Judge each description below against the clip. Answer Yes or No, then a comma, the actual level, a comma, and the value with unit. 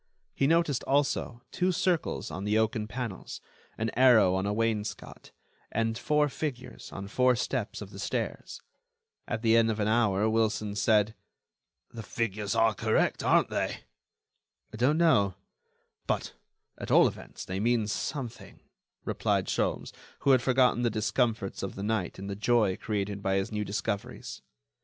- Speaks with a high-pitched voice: No, low, 110 Hz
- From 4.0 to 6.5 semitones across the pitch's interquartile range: No, average, 3.2 semitones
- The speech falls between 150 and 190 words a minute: Yes, average, 155 wpm